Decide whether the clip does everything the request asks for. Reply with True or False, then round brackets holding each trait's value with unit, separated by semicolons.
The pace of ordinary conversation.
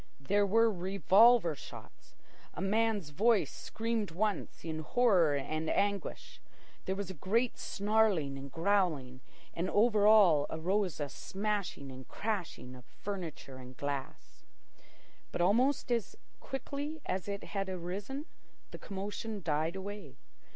False (130 wpm)